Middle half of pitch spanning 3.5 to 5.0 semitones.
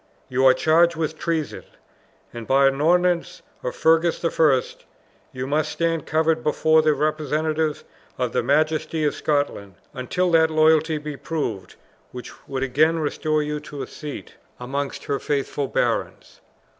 No: narrow, 2.6 semitones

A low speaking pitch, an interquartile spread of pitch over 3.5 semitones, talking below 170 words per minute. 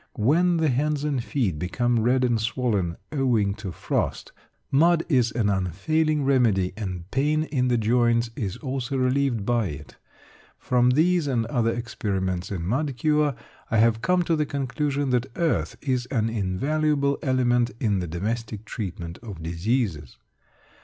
Yes: low, 120 Hz; average, 5.2 semitones; average, 155 wpm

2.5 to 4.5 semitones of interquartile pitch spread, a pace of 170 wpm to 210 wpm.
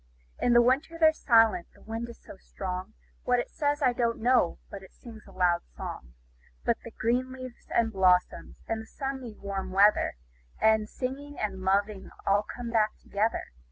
Yes: average, 3.9 semitones; average, 175 wpm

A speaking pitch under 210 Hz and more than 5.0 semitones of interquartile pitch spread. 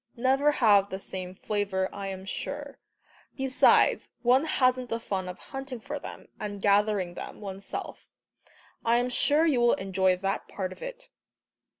No: high, 215 Hz; wide, 5.4 semitones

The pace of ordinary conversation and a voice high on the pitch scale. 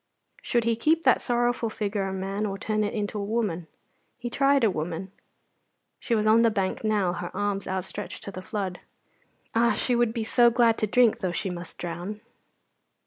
Yes: average, 195 wpm; high, 210 Hz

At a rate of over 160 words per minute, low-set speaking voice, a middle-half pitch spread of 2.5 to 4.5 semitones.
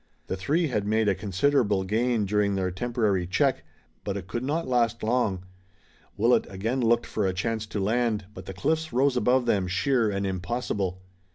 Yes: average, 180 wpm; low, 110 Hz; average, 4.2 semitones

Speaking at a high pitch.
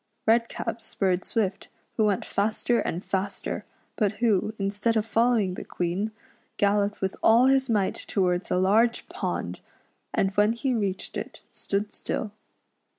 Yes: high, 210 Hz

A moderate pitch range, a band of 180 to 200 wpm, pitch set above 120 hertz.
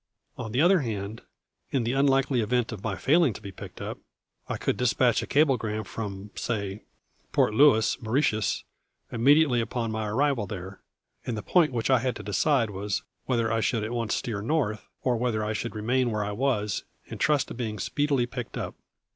No: average, 3.6 semitones; average, 190 wpm; low, 115 Hz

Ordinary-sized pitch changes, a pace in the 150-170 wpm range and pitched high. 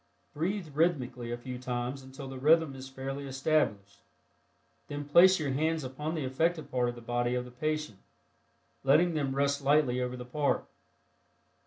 No: average, 3.6 semitones; average, 165 wpm; low, 135 Hz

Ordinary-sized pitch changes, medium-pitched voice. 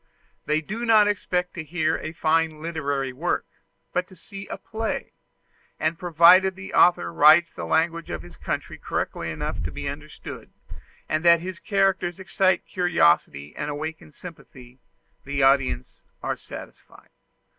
Yes: average, 3.8 semitones; medium, 165 Hz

